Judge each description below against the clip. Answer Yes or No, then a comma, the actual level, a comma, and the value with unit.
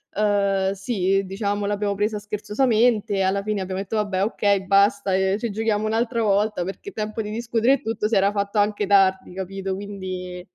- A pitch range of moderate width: No, narrow, 1.7 semitones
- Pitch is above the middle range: Yes, high, 205 Hz